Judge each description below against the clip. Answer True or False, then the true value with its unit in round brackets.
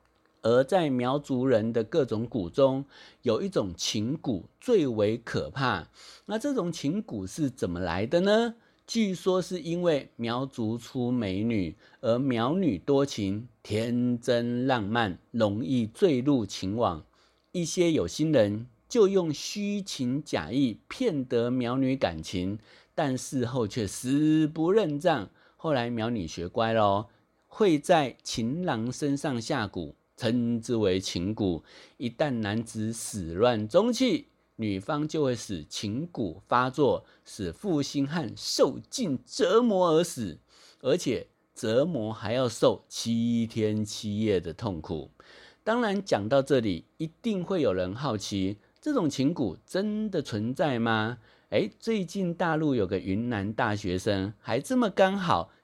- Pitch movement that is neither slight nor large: False (6.3 semitones)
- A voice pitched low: True (120 Hz)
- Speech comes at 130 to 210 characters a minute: True (195 characters per minute)